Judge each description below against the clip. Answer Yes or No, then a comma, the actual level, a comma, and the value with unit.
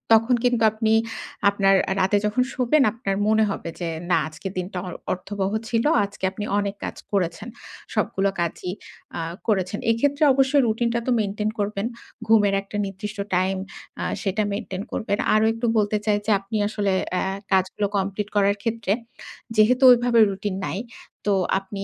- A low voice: No, high, 205 Hz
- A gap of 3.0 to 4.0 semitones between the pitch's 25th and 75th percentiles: No, narrow, 2.5 semitones